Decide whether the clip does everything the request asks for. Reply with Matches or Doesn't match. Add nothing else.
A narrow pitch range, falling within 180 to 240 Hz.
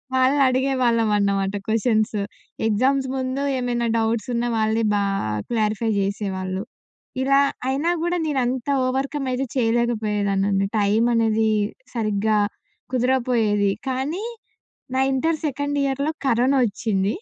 Doesn't match